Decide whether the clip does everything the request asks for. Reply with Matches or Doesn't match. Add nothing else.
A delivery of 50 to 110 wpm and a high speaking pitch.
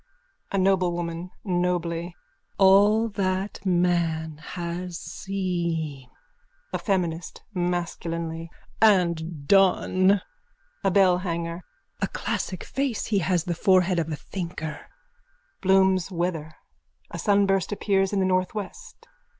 Doesn't match